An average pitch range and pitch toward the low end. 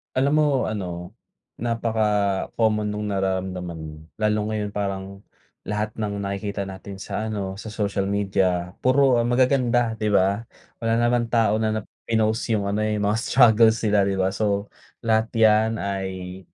No: narrow, 2.2 semitones; low, 105 Hz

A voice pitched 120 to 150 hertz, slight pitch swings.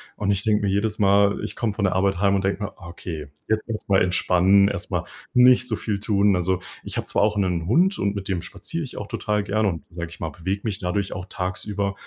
No: low, 100 Hz; narrow, 2.2 semitones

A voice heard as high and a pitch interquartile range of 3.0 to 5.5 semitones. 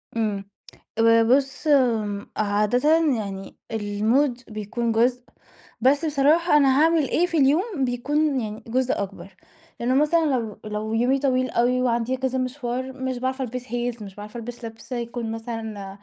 Yes: high, 245 Hz; average, 3.3 semitones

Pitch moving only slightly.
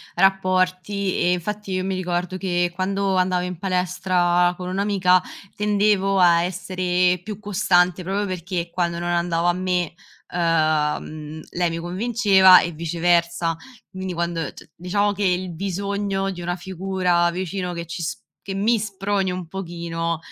Yes: narrow, 1.8 semitones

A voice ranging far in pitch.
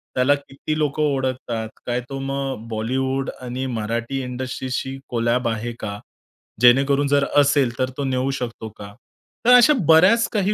No: average, 2.8 semitones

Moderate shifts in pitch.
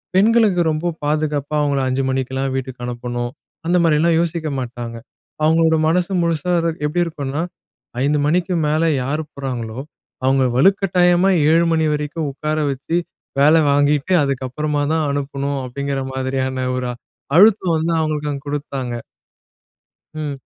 Yes: average, 3.7 semitones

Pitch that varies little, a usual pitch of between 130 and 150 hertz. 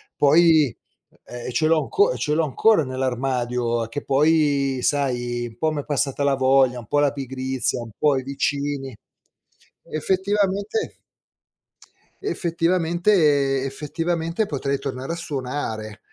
No: average, 3.8 semitones; medium, 140 Hz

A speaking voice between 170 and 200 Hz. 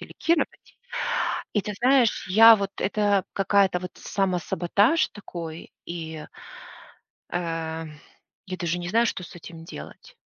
Yes: medium, 185 Hz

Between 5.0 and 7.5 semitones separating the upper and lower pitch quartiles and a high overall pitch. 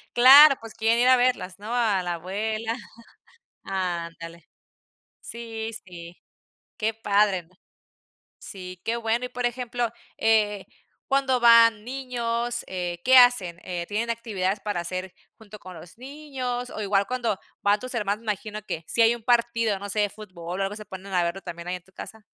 No: average, 4.2 semitones; high, 215 Hz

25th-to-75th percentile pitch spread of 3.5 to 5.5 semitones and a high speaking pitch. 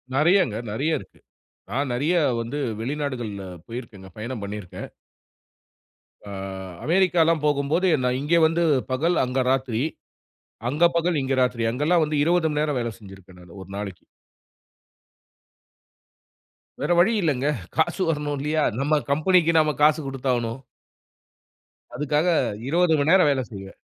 No: average, 5.2 semitones; medium, 145 Hz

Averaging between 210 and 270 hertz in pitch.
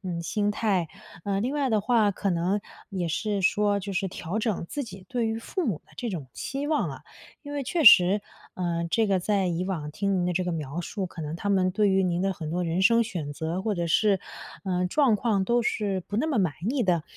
No: high, 195 Hz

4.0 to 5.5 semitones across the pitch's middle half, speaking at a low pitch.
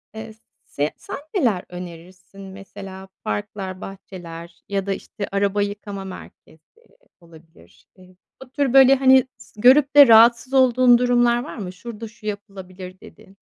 No: average, 4.4 semitones; high, 200 Hz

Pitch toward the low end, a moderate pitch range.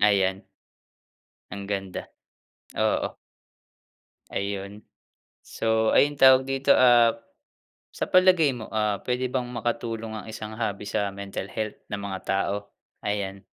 Yes: low, 110 Hz; average, 3.5 semitones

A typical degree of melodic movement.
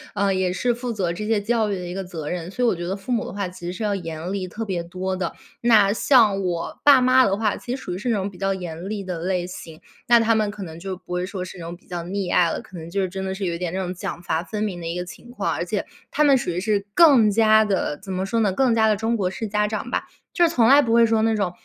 Yes: average, 3.8 semitones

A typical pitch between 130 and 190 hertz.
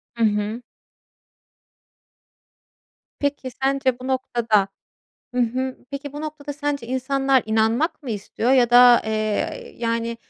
No: very high, 250 Hz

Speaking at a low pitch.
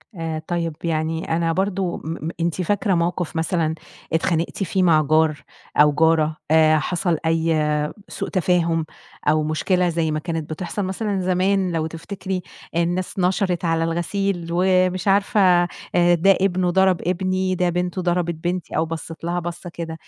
No: medium, 175 Hz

